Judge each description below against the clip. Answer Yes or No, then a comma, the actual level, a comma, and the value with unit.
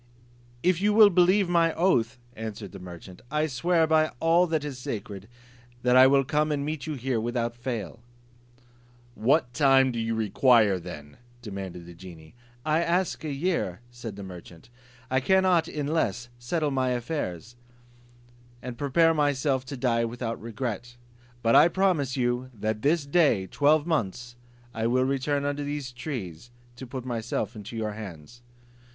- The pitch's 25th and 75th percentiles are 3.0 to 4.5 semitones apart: No, average, 5.2 semitones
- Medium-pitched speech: No, low, 130 Hz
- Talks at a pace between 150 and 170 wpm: Yes, average, 160 wpm